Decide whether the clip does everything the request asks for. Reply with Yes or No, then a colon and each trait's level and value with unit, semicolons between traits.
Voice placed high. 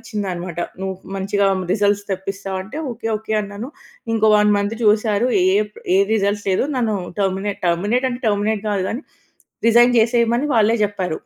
Yes: high, 205 Hz